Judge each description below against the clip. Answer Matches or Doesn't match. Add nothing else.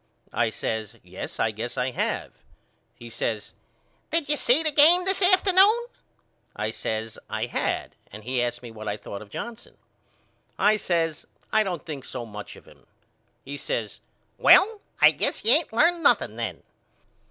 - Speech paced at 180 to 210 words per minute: Doesn't match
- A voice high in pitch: Doesn't match